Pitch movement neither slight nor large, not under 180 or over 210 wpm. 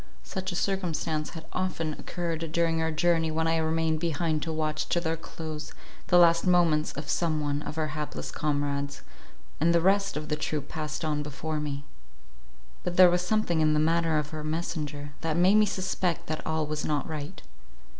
No: narrow, 2.0 semitones; average, 190 wpm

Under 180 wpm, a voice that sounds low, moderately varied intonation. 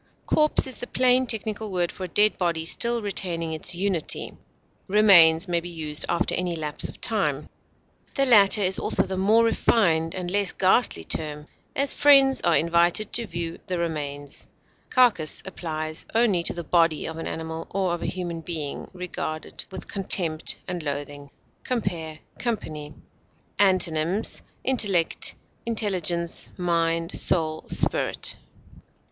No: average, 140 wpm; medium, 175 Hz; average, 4.0 semitones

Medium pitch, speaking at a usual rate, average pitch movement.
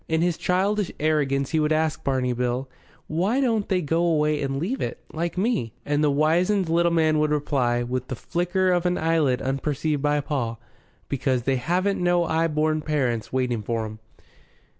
Yes: medium, 155 Hz; average, 180 wpm; average, 4.4 semitones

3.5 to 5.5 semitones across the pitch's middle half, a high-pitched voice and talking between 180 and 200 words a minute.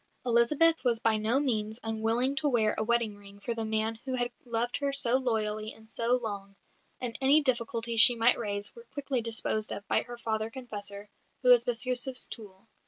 No: narrow, 2.4 semitones; high, 230 Hz; average, 190 wpm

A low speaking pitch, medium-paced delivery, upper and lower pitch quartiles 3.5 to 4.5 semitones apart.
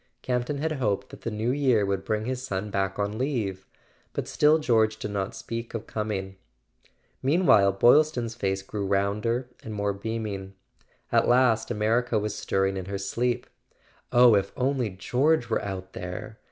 Yes: low, 110 Hz; average, 170 wpm; average, 3.9 semitones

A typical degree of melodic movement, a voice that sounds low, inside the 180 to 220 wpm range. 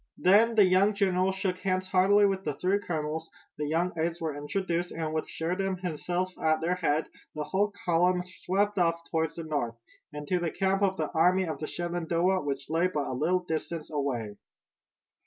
No: average, 3.0 semitones; medium, 175 Hz; average, 190 wpm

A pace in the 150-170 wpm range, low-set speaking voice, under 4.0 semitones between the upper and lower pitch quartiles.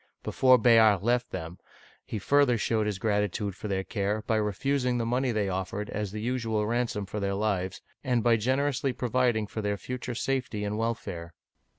No: average, 180 wpm; low, 110 Hz; average, 3.2 semitones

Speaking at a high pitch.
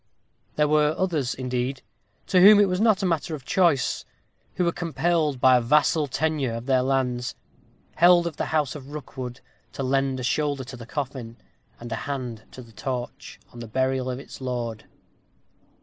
No: low, 135 Hz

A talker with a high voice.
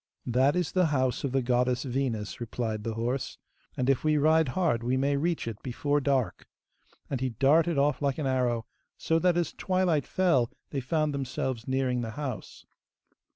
No: low, 135 Hz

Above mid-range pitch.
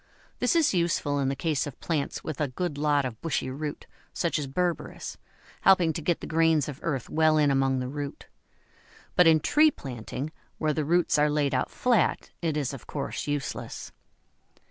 No: medium, 150 Hz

